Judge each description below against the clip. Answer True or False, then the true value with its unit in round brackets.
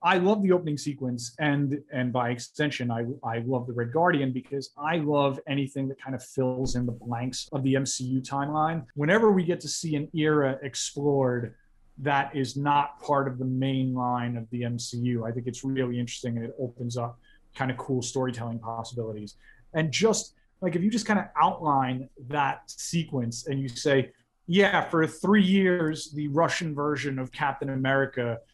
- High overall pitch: False (135 Hz)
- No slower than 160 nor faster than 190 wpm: True (185 wpm)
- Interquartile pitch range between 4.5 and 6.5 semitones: False (3.3 semitones)